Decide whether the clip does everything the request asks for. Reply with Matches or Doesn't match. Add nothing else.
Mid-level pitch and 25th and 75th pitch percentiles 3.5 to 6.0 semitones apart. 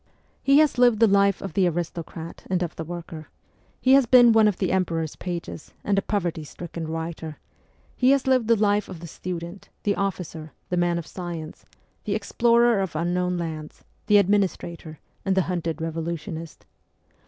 Matches